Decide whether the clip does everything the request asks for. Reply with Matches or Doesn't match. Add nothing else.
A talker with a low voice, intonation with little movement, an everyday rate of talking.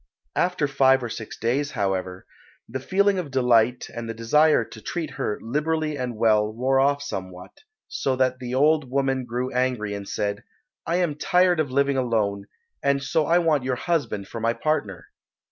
Doesn't match